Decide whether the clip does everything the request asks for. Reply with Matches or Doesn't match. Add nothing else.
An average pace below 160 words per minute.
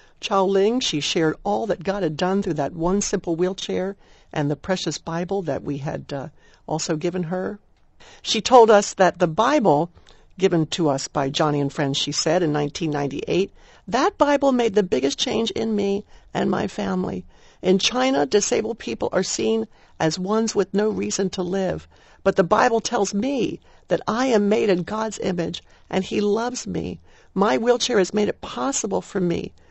Doesn't match